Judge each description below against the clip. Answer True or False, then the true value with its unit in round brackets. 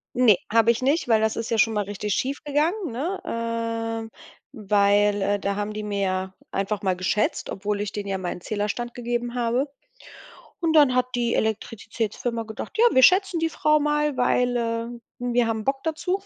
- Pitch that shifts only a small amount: False (3.5 semitones)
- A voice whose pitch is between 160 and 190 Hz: False (230 Hz)